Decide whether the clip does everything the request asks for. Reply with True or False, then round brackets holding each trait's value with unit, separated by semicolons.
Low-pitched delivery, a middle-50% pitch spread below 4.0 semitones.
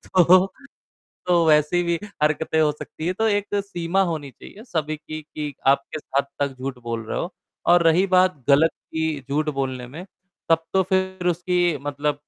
False (160 Hz; 3.4 semitones)